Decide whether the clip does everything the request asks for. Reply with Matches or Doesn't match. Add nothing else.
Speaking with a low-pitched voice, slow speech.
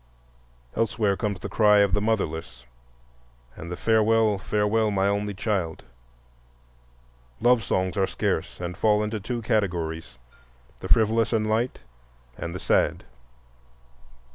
Matches